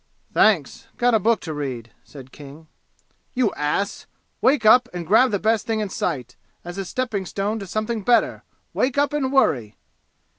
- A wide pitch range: Yes, wide, 7.5 semitones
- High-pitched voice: Yes, high, 205 Hz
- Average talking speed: Yes, average, 175 wpm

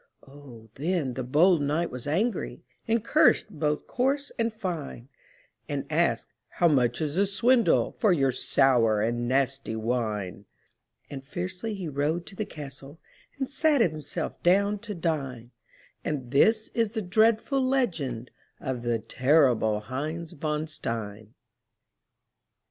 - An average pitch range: No, wide, 8.0 semitones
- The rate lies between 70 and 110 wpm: No, slow, 135 wpm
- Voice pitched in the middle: Yes, medium, 150 Hz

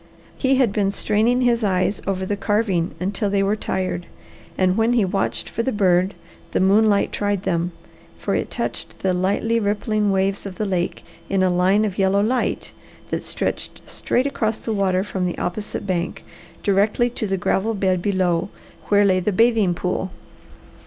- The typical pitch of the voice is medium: No, high, 200 Hz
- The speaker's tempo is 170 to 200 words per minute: Yes, average, 175 wpm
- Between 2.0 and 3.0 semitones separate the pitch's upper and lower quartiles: Yes, narrow, 2.4 semitones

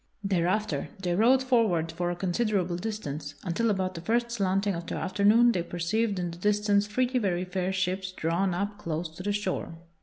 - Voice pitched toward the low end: No, high, 190 Hz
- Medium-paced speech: Yes, average, 185 wpm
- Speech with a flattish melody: No, average, 3.2 semitones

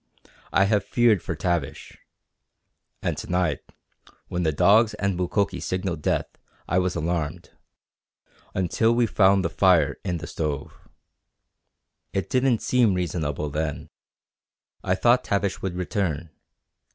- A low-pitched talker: Yes, very low, 90 Hz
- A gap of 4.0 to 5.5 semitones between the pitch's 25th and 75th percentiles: No, average, 3.6 semitones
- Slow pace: Yes, slow, 125 wpm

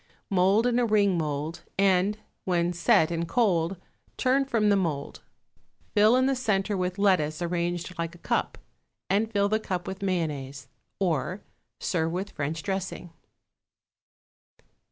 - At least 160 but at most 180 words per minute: No, average, 140 wpm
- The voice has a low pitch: No, medium, 185 Hz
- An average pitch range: Yes, average, 3.5 semitones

